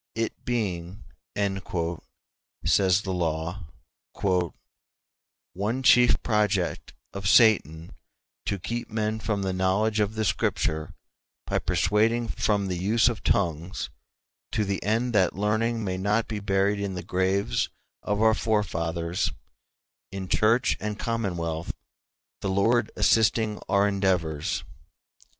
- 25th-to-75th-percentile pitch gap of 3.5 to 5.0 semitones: No, average, 3.0 semitones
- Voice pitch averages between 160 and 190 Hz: No, low, 100 Hz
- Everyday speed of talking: No, slow, 120 wpm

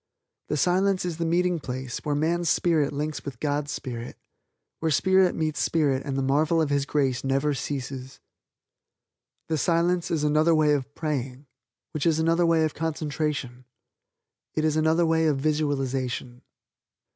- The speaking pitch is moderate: Yes, medium, 150 Hz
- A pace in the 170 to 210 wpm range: No, average, 155 wpm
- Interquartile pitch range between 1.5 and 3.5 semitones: Yes, average, 3.0 semitones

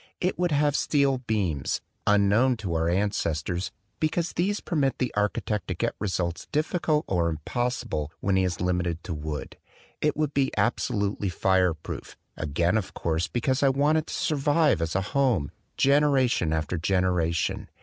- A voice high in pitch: No, low, 105 Hz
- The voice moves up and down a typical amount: No, wide, 8.3 semitones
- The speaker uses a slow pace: No, average, 160 wpm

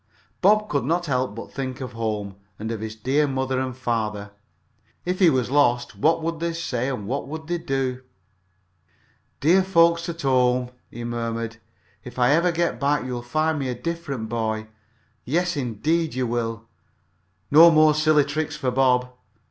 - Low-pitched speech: Yes, low, 130 Hz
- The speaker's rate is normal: Yes, average, 170 wpm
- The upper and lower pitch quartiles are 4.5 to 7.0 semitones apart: Yes, average, 5.0 semitones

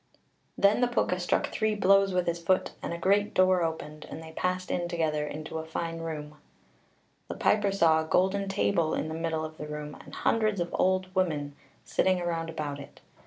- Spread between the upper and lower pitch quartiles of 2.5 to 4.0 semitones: Yes, average, 3.0 semitones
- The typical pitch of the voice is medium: Yes, medium, 170 Hz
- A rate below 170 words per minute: No, fast, 205 wpm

